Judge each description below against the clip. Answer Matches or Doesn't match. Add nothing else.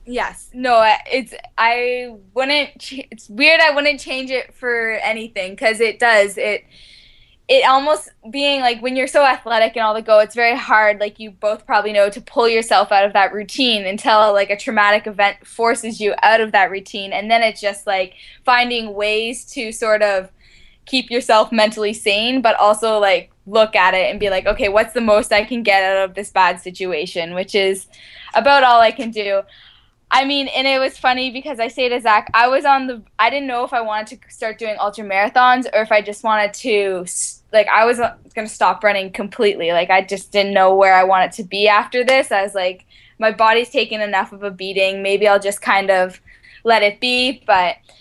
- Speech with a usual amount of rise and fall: Matches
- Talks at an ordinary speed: Doesn't match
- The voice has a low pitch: Doesn't match